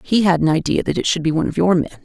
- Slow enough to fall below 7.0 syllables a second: No, 7.3 syllables/s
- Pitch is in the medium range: Yes, medium, 170 Hz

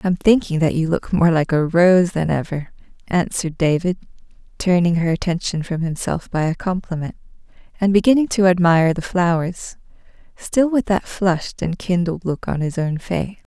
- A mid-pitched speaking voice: Yes, medium, 175 Hz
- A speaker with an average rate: Yes, average, 175 wpm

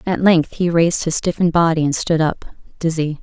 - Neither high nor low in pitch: Yes, medium, 165 Hz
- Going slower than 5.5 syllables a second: No, 5.8 syllables/s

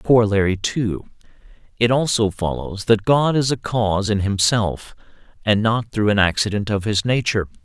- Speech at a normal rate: Yes, average, 150 wpm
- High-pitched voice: No, low, 105 Hz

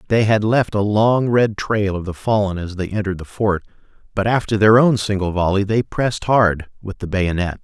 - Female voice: No, male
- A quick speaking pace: Yes, fast, 210 wpm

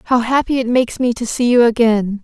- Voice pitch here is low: No, high, 240 Hz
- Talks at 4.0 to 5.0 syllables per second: No, 5.9 syllables/s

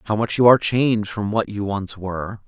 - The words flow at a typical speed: No, fast, 240 wpm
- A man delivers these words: Yes, male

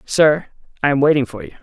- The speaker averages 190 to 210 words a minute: No, fast, 220 wpm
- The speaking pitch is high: No, medium, 145 Hz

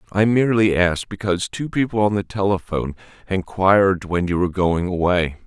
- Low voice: Yes, very low, 95 Hz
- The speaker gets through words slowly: No, average, 165 wpm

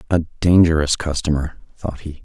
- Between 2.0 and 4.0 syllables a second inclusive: No, 5.2 syllables/s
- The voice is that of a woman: No, male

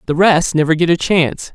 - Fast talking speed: Yes, fast, 235 wpm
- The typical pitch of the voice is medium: Yes, medium, 165 Hz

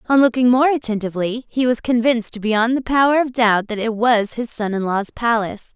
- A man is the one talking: No, female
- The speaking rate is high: Yes, fast, 210 wpm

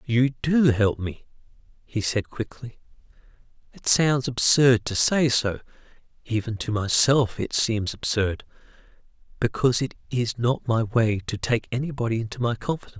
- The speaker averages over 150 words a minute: No, average, 145 wpm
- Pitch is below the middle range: Yes, low, 115 Hz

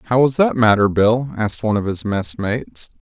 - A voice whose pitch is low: Yes, low, 110 Hz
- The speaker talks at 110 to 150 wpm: No, average, 200 wpm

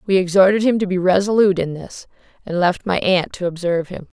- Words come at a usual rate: No, fast, 215 wpm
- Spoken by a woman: Yes, female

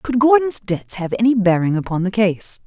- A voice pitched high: Yes, high, 210 Hz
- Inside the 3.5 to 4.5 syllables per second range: No, 5.0 syllables/s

